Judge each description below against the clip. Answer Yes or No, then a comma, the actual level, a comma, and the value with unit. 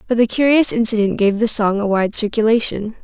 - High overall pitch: Yes, high, 220 Hz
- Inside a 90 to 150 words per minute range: No, average, 200 wpm